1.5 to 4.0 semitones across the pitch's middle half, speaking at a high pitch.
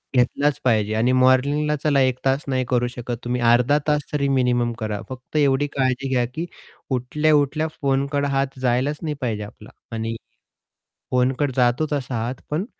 No: average, 2.7 semitones; low, 130 Hz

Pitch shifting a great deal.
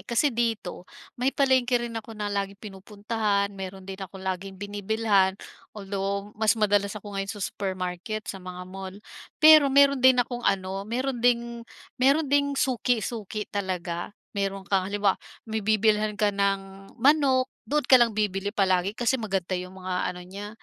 No: average, 3.5 semitones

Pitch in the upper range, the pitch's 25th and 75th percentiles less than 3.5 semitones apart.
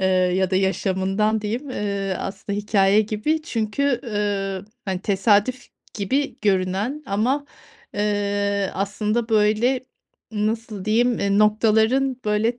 Yes: high, 210 Hz; average, 2.7 semitones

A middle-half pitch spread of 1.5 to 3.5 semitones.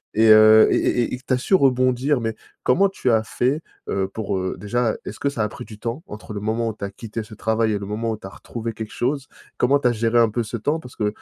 Yes: average, 2.7 semitones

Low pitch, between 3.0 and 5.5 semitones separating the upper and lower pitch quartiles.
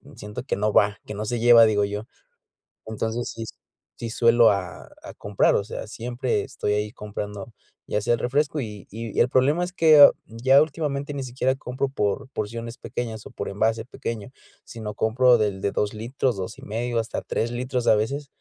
Yes: low, 115 Hz; average, 3.3 semitones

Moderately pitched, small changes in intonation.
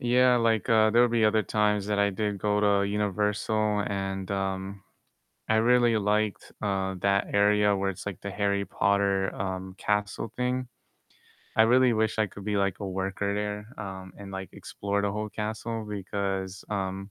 No: low, 100 Hz; narrow, 1.6 semitones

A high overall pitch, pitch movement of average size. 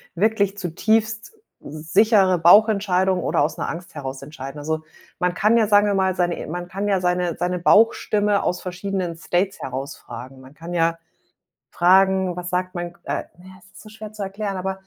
No: medium, 180 Hz; average, 3.0 semitones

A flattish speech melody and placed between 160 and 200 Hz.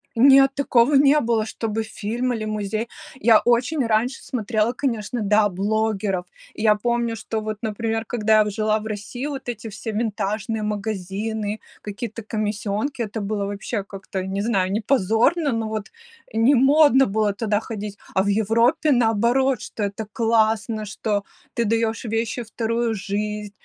No: narrow, 2.2 semitones; high, 220 Hz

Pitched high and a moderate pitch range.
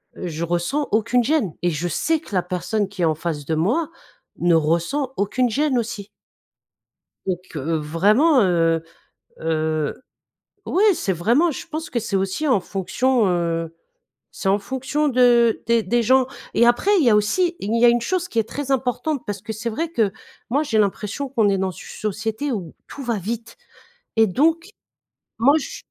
No: high, 220 Hz; wide, 6.6 semitones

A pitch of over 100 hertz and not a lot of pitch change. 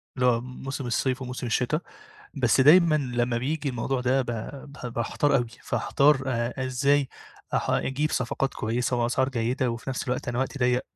Yes: low, 130 Hz; narrow, 2.0 semitones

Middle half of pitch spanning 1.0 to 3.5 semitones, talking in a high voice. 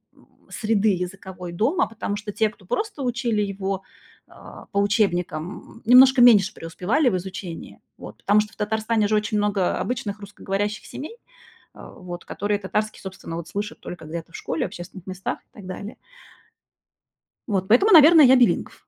Yes: average, 3.1 semitones; high, 205 Hz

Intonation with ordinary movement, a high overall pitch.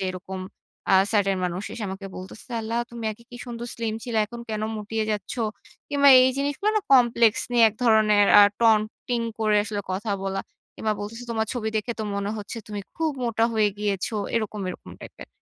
No: narrow, 2.3 semitones; high, 220 Hz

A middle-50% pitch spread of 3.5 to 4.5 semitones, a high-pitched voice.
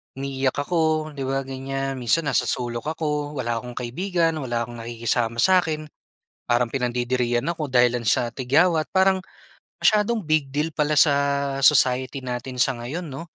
No: average, 4.1 semitones; low, 135 Hz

